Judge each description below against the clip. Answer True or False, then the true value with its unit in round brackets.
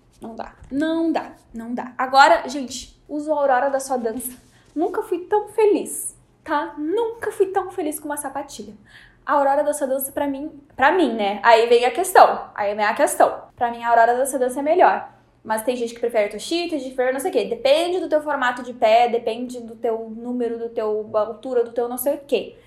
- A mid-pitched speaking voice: False (270 Hz)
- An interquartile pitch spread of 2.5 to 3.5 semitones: False (5.0 semitones)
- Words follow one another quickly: True (220 wpm)